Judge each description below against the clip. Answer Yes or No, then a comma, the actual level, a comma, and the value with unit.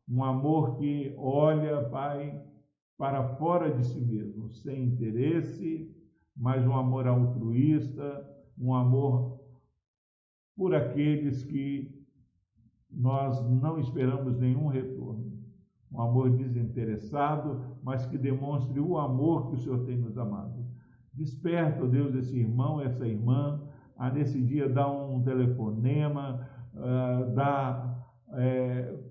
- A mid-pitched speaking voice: No, low, 130 Hz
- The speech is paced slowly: Yes, slow, 115 wpm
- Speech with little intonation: Yes, narrow, 2.3 semitones